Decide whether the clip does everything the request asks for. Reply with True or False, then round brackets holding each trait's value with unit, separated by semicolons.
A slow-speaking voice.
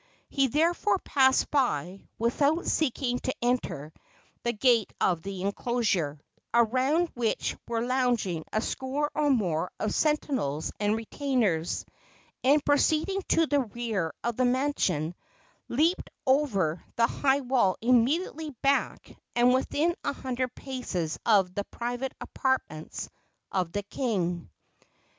True (125 wpm)